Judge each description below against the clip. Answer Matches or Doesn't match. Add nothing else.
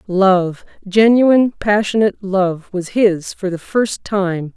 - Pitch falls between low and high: Doesn't match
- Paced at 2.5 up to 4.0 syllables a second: Matches